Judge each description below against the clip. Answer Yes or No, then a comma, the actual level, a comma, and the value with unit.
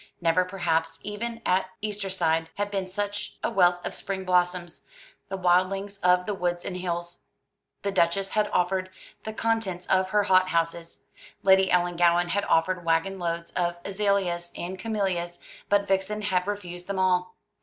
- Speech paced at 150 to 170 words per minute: Yes, average, 160 wpm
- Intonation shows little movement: Yes, narrow, 2.2 semitones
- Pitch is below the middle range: No, medium, 185 Hz